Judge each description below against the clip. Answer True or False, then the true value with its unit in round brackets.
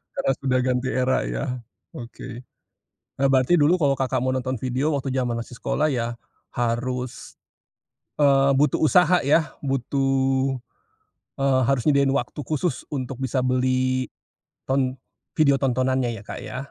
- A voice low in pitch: True (130 Hz)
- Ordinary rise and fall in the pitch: False (1.5 semitones)